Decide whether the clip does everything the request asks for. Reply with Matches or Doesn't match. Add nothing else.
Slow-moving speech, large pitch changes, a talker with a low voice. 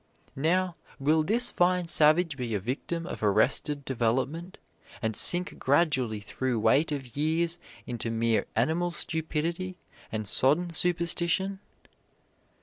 Doesn't match